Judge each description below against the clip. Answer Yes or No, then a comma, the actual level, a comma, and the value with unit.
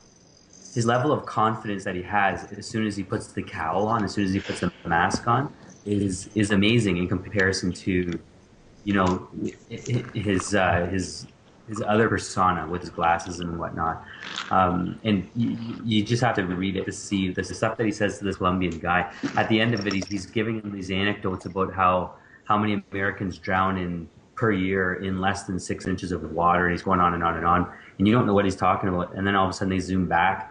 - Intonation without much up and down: Yes, narrow, 2.3 semitones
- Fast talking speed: Yes, fast, 225 wpm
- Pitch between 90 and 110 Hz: Yes, very low, 95 Hz